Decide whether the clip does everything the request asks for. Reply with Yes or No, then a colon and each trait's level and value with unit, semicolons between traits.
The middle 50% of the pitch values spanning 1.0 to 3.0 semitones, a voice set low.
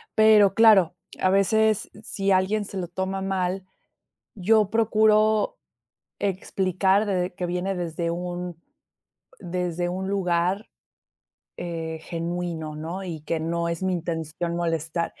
No: narrow, 2.6 semitones; medium, 180 Hz